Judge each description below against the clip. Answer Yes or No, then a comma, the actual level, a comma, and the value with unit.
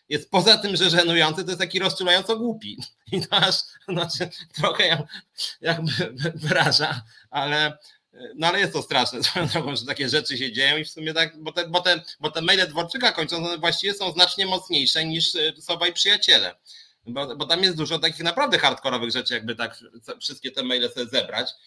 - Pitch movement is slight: No, average, 3.5 semitones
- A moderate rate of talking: No, fast, 180 wpm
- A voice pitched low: No, medium, 170 Hz